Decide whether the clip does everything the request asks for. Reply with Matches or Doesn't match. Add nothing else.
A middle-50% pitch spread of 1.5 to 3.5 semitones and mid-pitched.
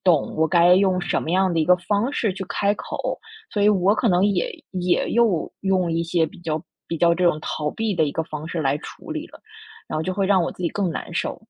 Matches